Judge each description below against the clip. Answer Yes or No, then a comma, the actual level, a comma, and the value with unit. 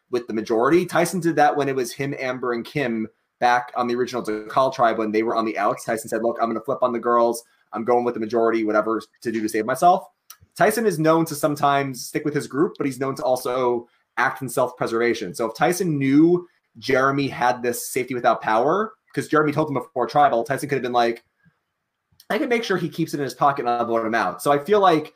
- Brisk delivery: Yes, fast, 250 wpm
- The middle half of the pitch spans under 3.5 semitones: No, average, 4.1 semitones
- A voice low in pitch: Yes, low, 125 Hz